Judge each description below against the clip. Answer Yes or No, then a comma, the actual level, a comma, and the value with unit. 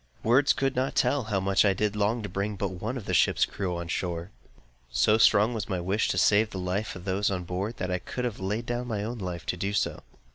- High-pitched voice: No, low, 100 Hz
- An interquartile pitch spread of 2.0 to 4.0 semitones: Yes, average, 3.3 semitones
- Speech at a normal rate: No, fast, 260 wpm